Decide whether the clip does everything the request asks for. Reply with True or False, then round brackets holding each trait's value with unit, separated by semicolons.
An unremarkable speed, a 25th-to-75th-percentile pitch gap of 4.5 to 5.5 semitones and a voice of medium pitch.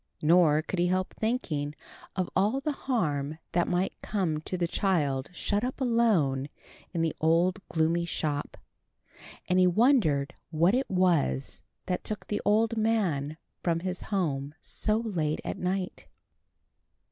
True (145 wpm; 5.1 semitones; 180 Hz)